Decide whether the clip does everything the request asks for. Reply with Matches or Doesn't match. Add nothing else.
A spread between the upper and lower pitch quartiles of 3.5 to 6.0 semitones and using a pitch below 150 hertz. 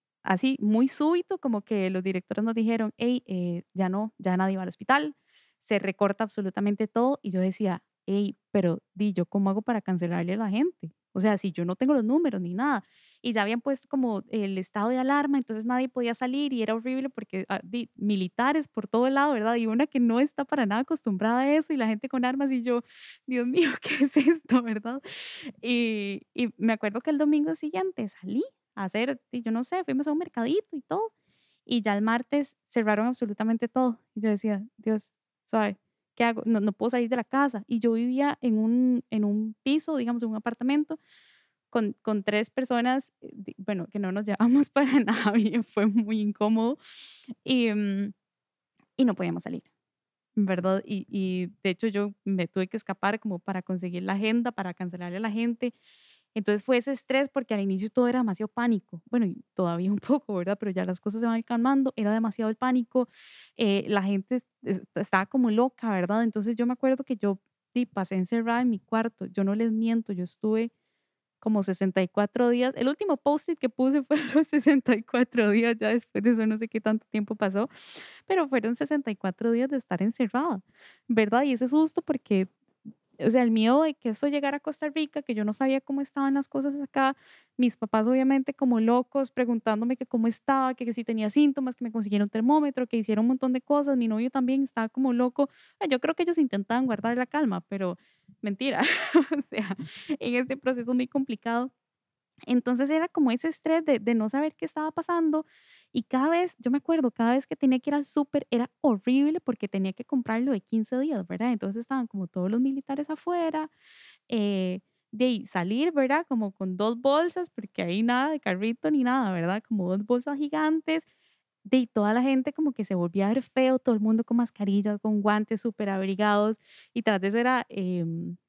Doesn't match